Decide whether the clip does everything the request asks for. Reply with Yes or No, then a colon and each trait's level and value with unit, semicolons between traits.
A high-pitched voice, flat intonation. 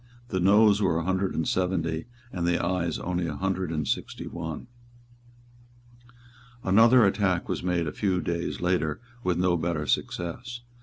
No: very low, 90 Hz; narrow, 2.3 semitones